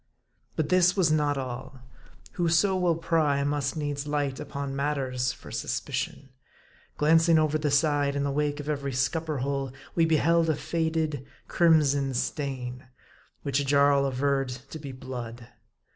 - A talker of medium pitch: Yes, medium, 145 Hz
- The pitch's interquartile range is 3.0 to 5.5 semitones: No, narrow, 2.6 semitones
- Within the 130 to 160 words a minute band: Yes, average, 145 wpm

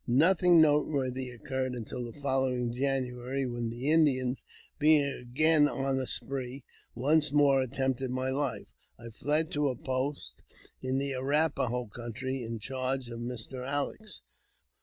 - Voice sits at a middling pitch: No, low, 130 Hz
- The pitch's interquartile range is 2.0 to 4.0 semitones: Yes, narrow, 2.4 semitones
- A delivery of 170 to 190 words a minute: No, average, 145 wpm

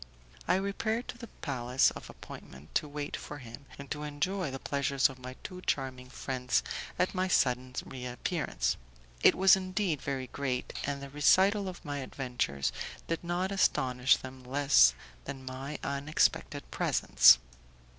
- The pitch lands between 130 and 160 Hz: Yes, medium, 140 Hz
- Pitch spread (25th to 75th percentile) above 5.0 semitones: Yes, wide, 5.4 semitones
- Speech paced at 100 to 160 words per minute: Yes, average, 150 wpm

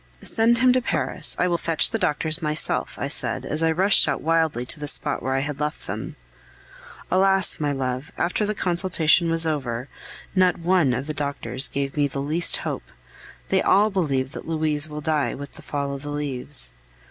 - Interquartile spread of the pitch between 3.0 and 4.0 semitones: Yes, average, 3.6 semitones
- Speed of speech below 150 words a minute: No, average, 195 wpm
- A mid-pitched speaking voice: Yes, medium, 155 Hz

